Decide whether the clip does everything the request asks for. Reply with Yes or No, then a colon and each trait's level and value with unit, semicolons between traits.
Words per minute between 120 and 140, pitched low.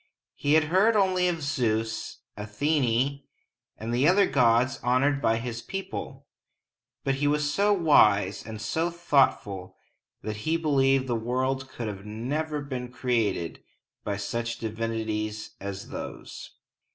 Yes: slow, 135 wpm; low, 125 Hz